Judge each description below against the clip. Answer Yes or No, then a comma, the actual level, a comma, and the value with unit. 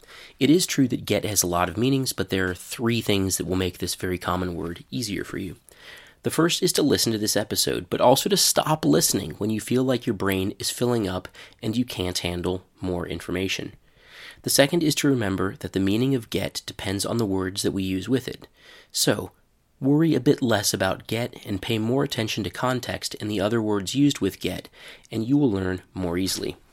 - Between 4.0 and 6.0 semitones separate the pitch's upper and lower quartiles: Yes, average, 5.2 semitones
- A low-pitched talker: Yes, low, 105 Hz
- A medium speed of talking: No, fast, 220 wpm